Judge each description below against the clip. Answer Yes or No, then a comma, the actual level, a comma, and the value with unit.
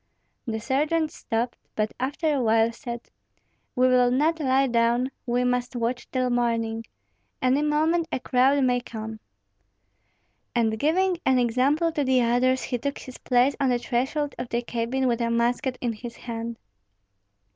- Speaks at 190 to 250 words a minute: No, average, 160 wpm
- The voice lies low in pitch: No, very high, 250 Hz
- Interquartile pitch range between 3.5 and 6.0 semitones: No, narrow, 2.6 semitones